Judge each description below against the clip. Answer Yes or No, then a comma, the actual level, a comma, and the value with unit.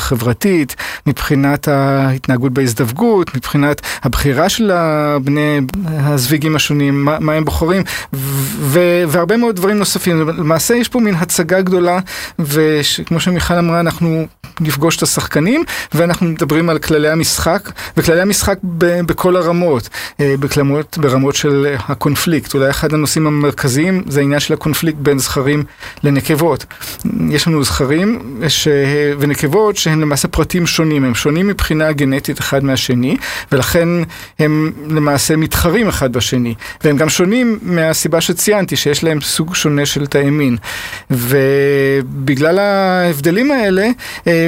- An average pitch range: Yes, average, 3.4 semitones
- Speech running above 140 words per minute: No, average, 125 wpm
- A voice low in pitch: No, medium, 155 Hz